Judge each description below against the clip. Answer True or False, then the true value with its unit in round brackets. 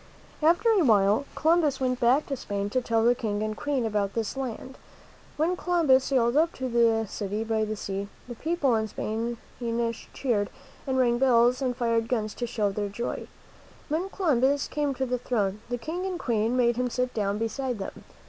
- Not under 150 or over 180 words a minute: False (190 wpm)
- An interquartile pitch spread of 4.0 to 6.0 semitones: False (3.6 semitones)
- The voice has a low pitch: False (240 Hz)